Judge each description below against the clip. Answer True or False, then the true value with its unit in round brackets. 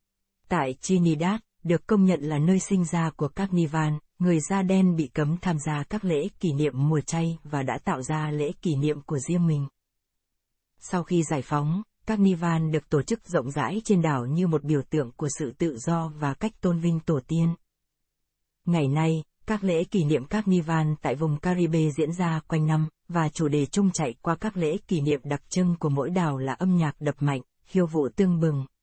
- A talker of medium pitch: True (165 Hz)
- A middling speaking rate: True (210 wpm)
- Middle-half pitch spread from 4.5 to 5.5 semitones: False (3.2 semitones)